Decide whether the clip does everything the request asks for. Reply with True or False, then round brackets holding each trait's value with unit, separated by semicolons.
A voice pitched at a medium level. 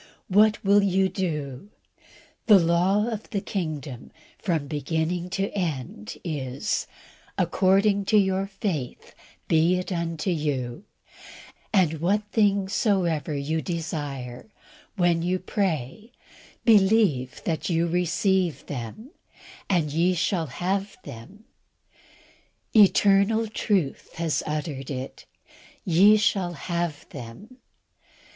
True (175 Hz)